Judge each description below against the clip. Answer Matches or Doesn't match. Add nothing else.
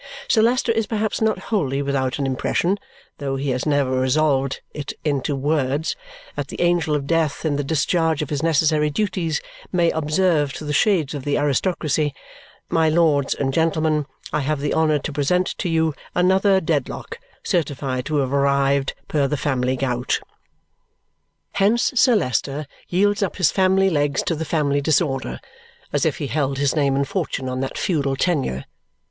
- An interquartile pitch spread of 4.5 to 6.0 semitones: Doesn't match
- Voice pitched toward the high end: Doesn't match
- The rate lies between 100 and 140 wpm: Doesn't match